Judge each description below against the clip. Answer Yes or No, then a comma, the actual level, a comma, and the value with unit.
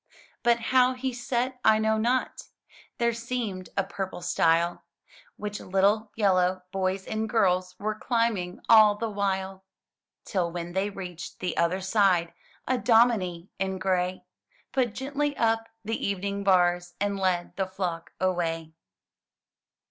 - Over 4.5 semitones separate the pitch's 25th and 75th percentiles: No, average, 3.7 semitones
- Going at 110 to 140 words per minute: Yes, slow, 135 wpm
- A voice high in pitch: Yes, high, 195 Hz